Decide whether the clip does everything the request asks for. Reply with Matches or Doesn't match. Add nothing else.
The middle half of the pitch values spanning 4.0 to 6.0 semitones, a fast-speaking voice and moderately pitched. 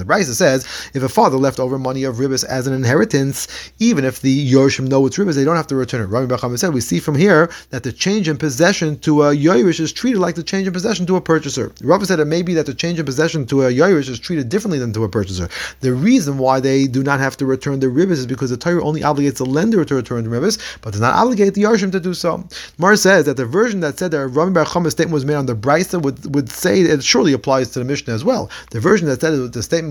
Matches